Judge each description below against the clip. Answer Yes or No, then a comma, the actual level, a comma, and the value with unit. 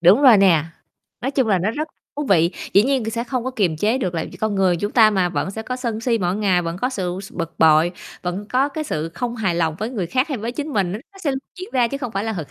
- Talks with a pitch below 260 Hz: Yes, high, 215 Hz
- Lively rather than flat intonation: Yes, wide, 6.0 semitones